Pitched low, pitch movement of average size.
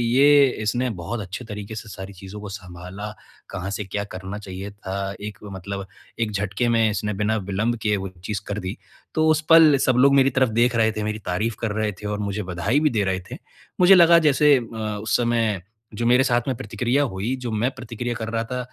Yes: low, 110 Hz; average, 3.5 semitones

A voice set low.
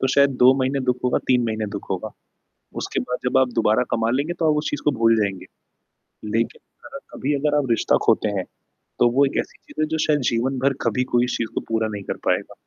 Yes: low, 125 Hz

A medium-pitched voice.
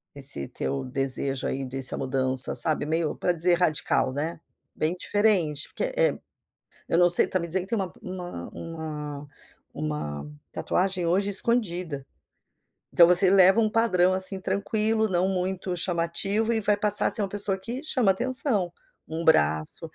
Yes: medium, 180 Hz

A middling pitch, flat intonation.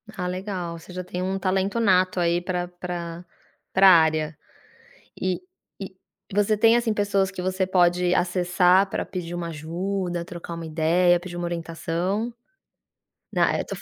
Yes: medium, 180 Hz; narrow, 1.8 semitones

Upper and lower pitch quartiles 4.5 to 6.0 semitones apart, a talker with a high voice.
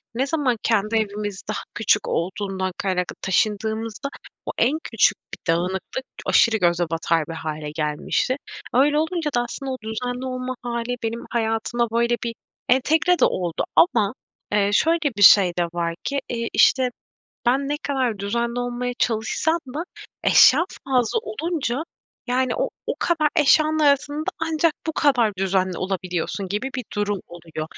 Yes: wide, 5.5 semitones; high, 235 Hz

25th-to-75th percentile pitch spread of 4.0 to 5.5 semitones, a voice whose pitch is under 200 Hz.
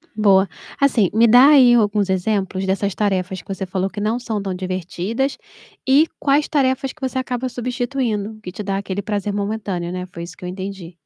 No: average, 4.4 semitones; high, 205 Hz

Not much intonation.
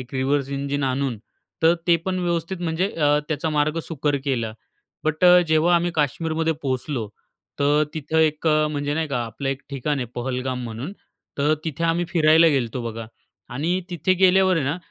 No: average, 3.5 semitones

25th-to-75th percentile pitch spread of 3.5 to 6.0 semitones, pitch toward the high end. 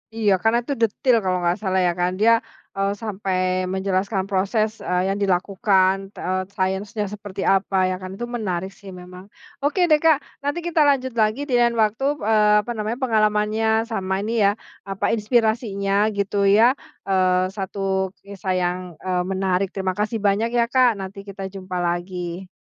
No: average, 2.9 semitones; high, 200 Hz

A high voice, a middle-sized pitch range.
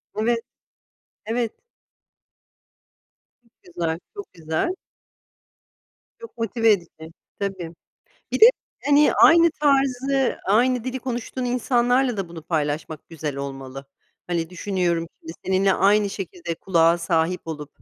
No: high, 195 Hz; wide, 7.1 semitones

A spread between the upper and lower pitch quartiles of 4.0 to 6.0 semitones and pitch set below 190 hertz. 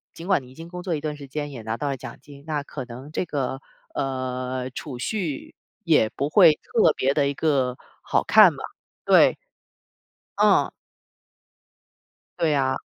No: average, 3.2 semitones; medium, 140 Hz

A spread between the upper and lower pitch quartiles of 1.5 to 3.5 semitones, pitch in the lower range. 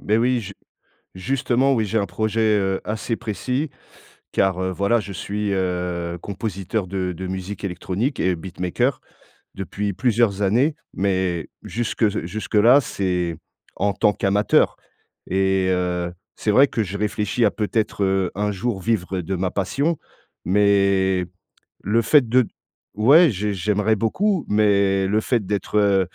Yes: average, 2.9 semitones; low, 100 Hz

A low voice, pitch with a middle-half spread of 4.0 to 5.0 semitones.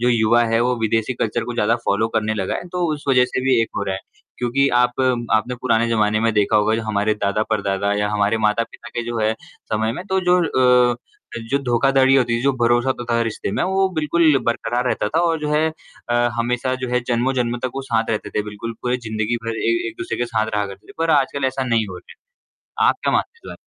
No: low, 120 Hz; average, 3.3 semitones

